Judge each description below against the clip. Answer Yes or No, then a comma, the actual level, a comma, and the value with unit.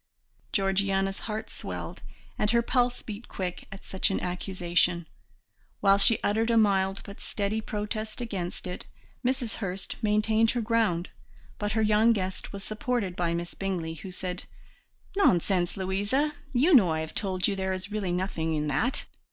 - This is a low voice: No, high, 195 Hz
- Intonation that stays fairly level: No, average, 3.2 semitones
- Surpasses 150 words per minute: Yes, average, 160 wpm